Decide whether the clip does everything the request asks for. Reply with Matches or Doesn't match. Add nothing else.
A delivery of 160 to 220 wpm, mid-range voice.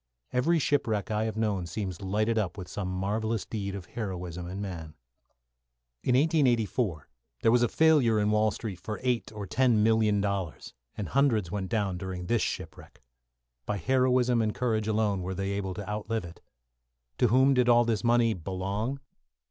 Doesn't match